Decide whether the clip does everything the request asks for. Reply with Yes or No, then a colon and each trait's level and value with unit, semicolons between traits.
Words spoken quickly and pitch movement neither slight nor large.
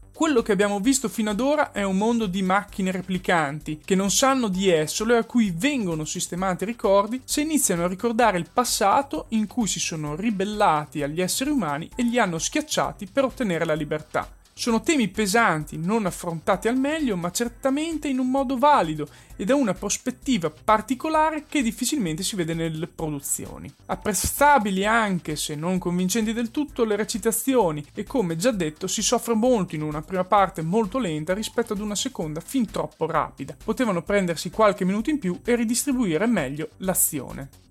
No: fast, 175 wpm; wide, 5.8 semitones